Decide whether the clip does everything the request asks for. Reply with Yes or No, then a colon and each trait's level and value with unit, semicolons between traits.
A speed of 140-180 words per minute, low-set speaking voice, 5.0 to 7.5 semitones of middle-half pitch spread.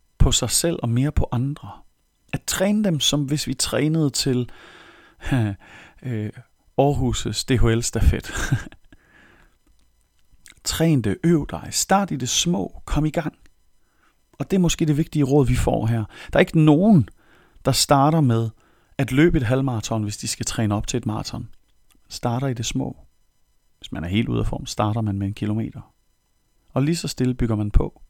Yes: average, 170 wpm; low, 125 Hz; average, 5.3 semitones